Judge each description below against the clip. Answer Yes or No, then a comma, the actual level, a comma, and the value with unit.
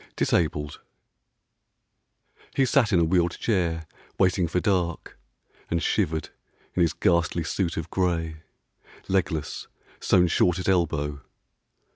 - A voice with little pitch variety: Yes, narrow, 2.2 semitones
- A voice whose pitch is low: Yes, very low, 85 Hz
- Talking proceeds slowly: Yes, slow, 115 wpm